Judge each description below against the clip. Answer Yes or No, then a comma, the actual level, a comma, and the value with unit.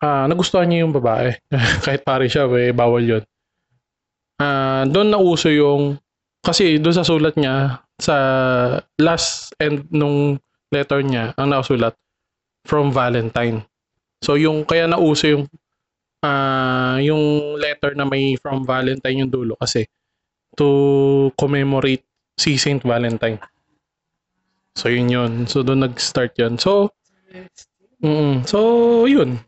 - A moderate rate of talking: Yes, average, 130 wpm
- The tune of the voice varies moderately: Yes, average, 3.6 semitones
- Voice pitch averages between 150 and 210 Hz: No, medium, 140 Hz